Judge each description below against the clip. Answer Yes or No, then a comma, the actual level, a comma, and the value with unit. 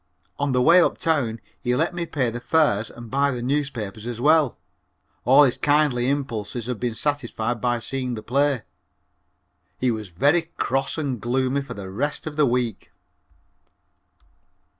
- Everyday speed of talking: Yes, average, 160 wpm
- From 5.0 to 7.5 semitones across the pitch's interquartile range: No, average, 3.4 semitones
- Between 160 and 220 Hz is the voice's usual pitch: No, low, 130 Hz